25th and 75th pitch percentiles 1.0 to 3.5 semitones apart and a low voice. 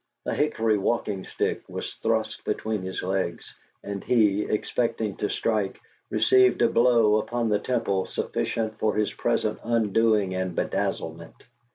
Yes: average, 2.7 semitones; low, 110 Hz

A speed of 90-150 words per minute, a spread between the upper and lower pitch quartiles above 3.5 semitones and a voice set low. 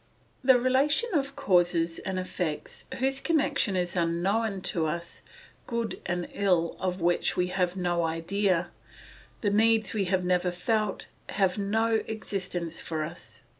No: average, 140 wpm; average, 4.2 semitones; medium, 185 Hz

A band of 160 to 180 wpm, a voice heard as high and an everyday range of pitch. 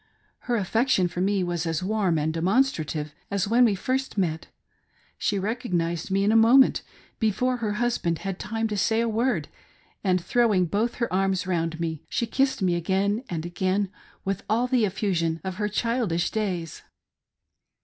Yes: average, 175 wpm; high, 195 Hz; average, 4.6 semitones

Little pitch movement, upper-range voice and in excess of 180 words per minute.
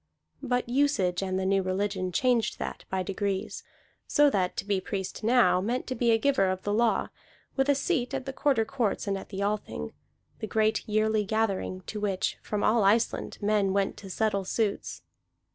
No: average, 3.5 semitones; high, 210 Hz; average, 190 wpm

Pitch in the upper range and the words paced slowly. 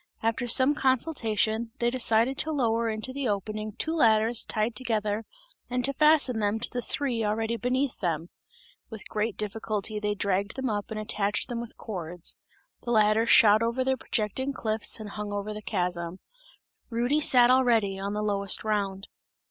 No: high, 220 Hz; average, 170 wpm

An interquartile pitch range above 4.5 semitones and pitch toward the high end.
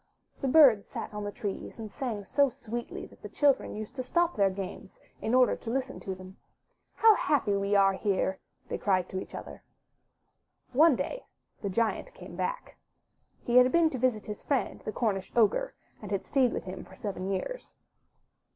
Yes: average, 5.1 semitones; high, 225 Hz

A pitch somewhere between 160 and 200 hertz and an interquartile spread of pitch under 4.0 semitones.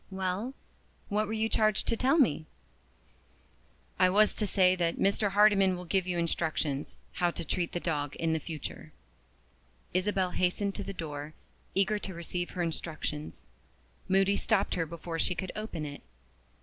Yes: medium, 185 Hz; average, 3.3 semitones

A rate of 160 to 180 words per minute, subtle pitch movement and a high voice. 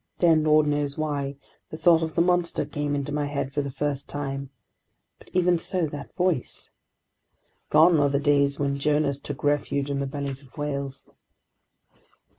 No: average, 170 wpm; narrow, 1.9 semitones; medium, 145 Hz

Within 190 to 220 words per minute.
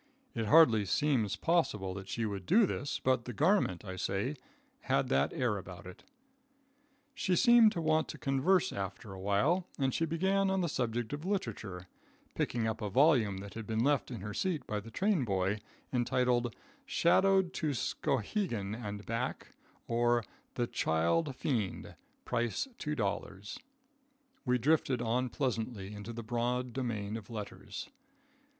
No: average, 150 wpm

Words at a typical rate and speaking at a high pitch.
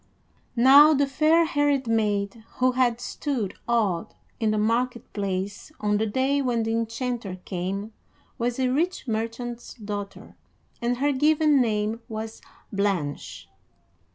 No: slow, 130 wpm; high, 230 Hz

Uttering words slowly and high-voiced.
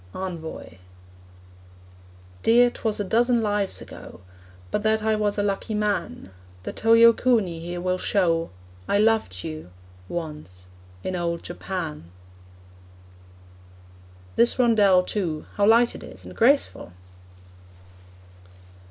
Yes: slow, 110 wpm; high, 200 Hz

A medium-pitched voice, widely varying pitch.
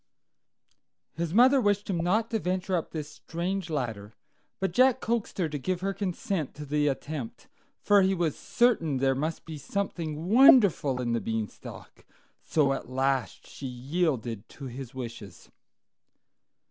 Yes: medium, 160 Hz; wide, 6.4 semitones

